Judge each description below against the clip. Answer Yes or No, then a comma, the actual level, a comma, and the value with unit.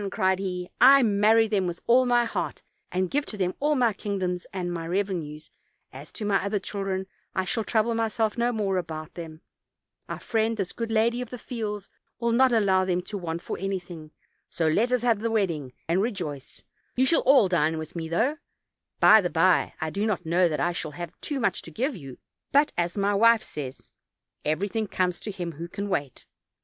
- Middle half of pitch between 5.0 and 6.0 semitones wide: No, average, 4.5 semitones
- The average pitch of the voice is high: Yes, high, 195 Hz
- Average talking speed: No, fast, 210 wpm